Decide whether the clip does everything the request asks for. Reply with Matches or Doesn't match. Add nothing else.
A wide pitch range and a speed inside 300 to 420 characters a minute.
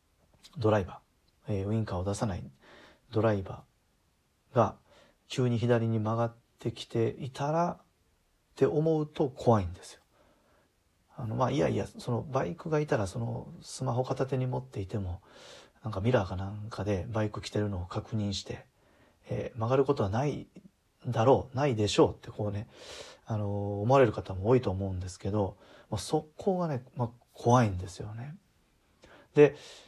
Doesn't match